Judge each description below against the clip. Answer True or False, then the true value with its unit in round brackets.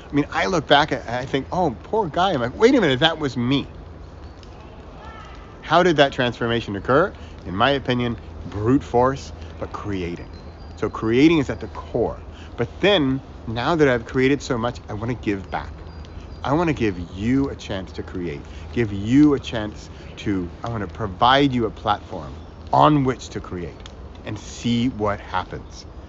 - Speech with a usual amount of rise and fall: False (7.2 semitones)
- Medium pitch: False (105 Hz)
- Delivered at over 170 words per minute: True (180 wpm)